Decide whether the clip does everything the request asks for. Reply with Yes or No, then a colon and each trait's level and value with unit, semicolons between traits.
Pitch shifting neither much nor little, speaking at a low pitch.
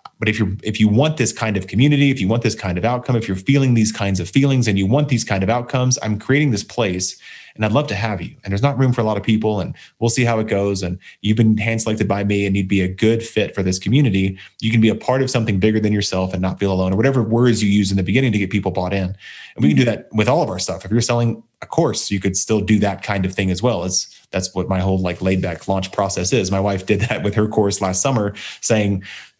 Yes: average, 3.3 semitones; low, 105 Hz